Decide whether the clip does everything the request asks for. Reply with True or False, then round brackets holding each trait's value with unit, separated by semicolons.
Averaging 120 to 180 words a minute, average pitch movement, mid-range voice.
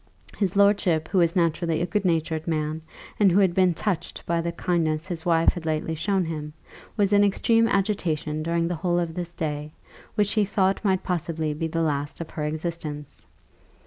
False (190 wpm; 3.1 semitones; 170 Hz)